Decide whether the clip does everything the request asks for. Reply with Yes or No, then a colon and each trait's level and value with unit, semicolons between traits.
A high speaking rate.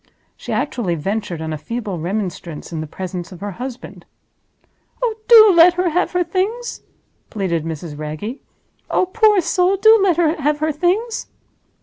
No: average, 160 wpm